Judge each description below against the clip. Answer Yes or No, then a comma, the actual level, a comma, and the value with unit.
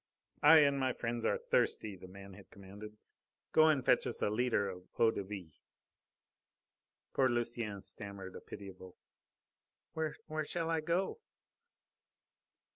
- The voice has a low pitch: Yes, low, 110 Hz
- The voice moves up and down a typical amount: No, wide, 5.9 semitones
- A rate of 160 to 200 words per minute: No, slow, 135 wpm